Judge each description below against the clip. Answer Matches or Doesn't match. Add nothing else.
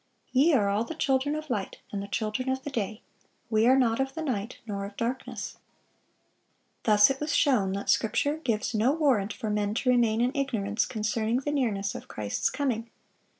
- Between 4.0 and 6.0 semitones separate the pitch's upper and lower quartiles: Matches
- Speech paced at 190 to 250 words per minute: Matches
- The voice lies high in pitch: Matches